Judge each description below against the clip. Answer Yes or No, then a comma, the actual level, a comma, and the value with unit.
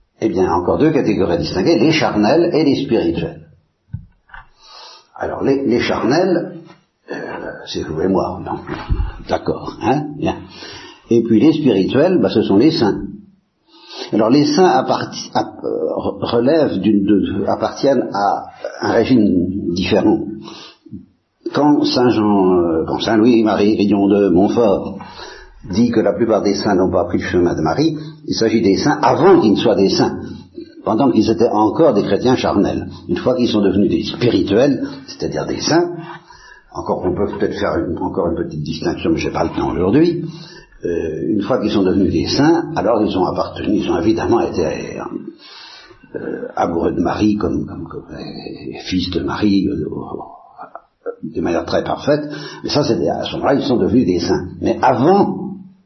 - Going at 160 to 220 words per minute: Yes, fast, 170 wpm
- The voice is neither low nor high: No, low, 120 Hz